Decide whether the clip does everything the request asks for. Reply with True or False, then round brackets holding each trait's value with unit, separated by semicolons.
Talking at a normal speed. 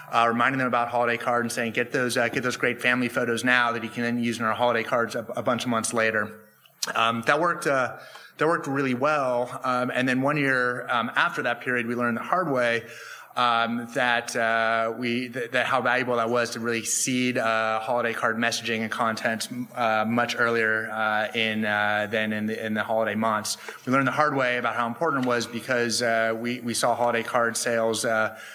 False (220 wpm)